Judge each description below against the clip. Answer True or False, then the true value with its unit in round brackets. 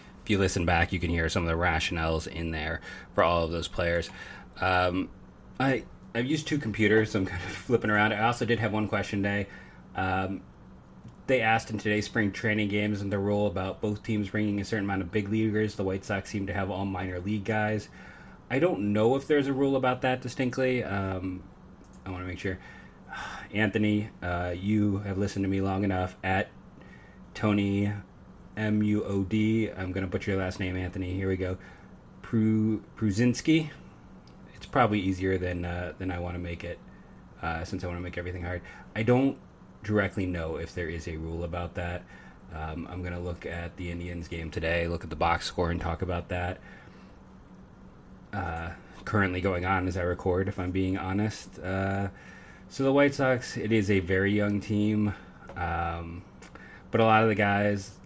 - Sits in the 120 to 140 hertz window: False (95 Hz)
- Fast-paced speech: False (195 wpm)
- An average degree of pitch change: True (3.1 semitones)